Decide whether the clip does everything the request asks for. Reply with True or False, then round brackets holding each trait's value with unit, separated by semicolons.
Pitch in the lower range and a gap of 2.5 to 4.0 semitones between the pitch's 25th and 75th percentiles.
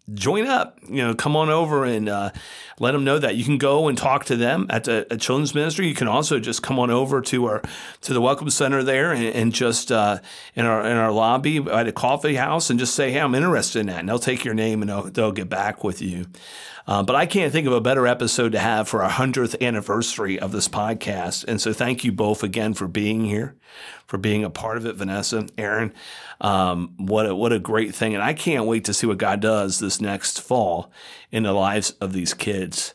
True (115 Hz; 3.7 semitones)